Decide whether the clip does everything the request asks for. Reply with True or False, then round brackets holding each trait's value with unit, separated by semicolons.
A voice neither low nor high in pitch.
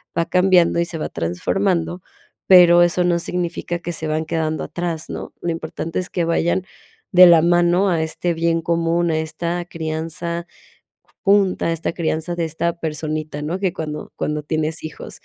True (170 Hz)